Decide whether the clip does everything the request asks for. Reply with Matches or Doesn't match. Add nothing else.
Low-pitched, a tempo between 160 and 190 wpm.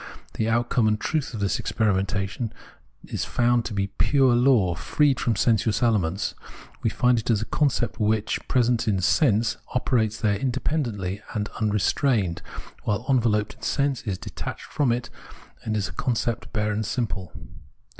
Matches